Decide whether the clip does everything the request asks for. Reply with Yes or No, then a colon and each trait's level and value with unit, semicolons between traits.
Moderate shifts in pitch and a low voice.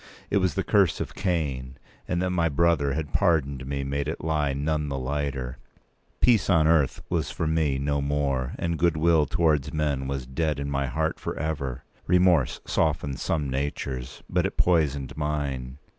Yes: average, 3.1 semitones; very low, 75 Hz